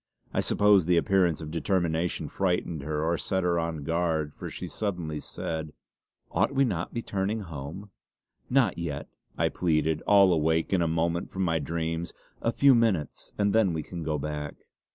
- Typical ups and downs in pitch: Yes, average, 3.4 semitones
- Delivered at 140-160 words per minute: No, average, 180 wpm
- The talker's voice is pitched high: No, very low, 85 Hz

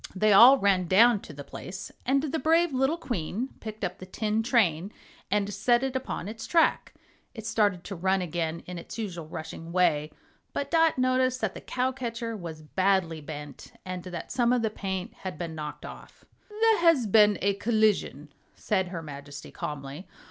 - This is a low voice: No, high, 200 Hz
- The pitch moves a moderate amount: No, wide, 6.1 semitones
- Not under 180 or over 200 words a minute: Yes, average, 185 wpm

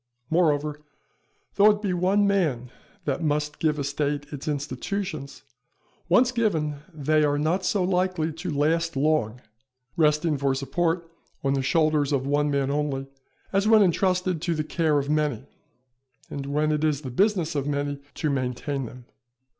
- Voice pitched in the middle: Yes, medium, 150 Hz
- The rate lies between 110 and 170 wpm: Yes, average, 160 wpm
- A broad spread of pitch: No, average, 3.4 semitones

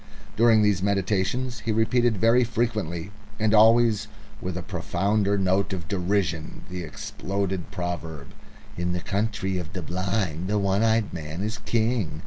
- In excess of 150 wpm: No, average, 145 wpm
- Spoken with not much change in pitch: No, average, 3.7 semitones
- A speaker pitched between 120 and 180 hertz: No, low, 100 Hz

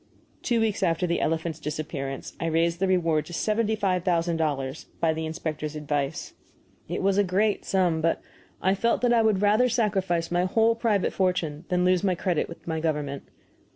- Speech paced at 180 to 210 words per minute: Yes, average, 190 wpm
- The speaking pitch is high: No, medium, 175 Hz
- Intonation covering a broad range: No, average, 3.7 semitones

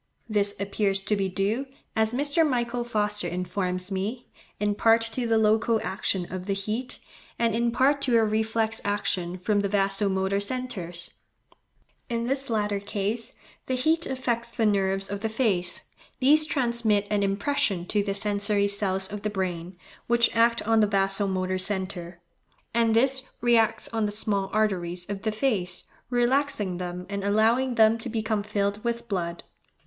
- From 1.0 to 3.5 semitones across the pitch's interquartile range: Yes, average, 3.1 semitones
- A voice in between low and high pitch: No, high, 210 Hz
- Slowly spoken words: No, average, 165 wpm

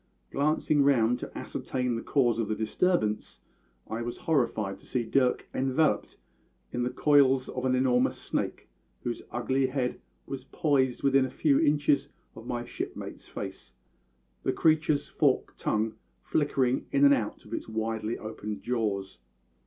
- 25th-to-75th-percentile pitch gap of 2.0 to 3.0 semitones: No, average, 3.7 semitones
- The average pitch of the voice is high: No, low, 125 Hz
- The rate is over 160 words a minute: No, average, 150 wpm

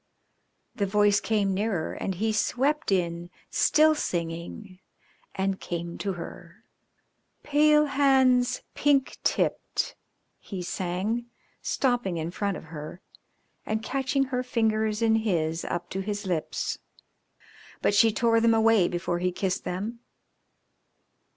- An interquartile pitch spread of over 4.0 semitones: Yes, average, 5.0 semitones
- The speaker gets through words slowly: Yes, slow, 125 wpm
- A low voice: No, high, 205 Hz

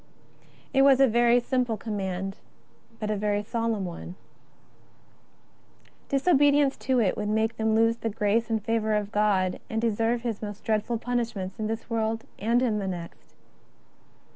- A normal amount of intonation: No, narrow, 2.2 semitones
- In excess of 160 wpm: No, average, 150 wpm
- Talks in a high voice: Yes, high, 220 Hz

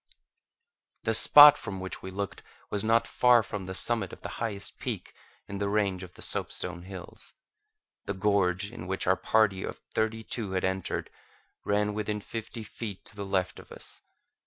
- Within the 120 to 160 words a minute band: No, average, 180 wpm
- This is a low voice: Yes, low, 100 Hz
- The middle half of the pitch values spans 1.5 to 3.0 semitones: Yes, narrow, 2.6 semitones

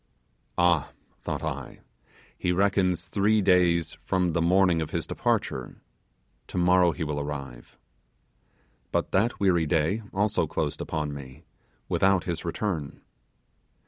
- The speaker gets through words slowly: Yes, slow, 120 wpm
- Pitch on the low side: Yes, very low, 85 Hz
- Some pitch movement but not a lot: Yes, average, 3.2 semitones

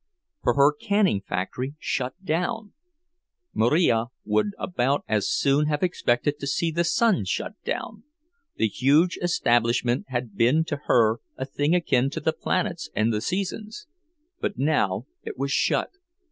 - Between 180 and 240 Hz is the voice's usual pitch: No, medium, 140 Hz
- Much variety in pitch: Yes, wide, 6.8 semitones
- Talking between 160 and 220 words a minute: No, average, 145 wpm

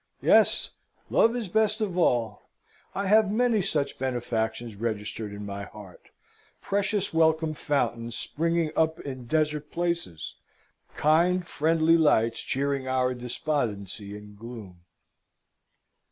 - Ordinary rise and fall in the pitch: No, wide, 6.9 semitones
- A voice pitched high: No, medium, 140 Hz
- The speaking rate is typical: No, slow, 115 wpm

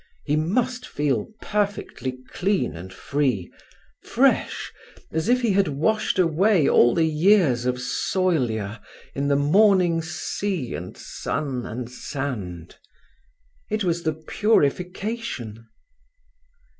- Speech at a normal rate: No, slow, 105 wpm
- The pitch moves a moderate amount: No, wide, 7.6 semitones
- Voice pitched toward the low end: No, medium, 155 Hz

